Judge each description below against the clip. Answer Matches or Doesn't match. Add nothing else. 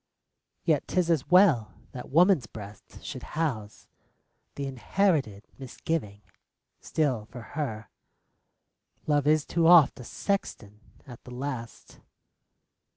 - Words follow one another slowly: Matches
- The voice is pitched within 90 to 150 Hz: Matches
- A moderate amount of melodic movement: Doesn't match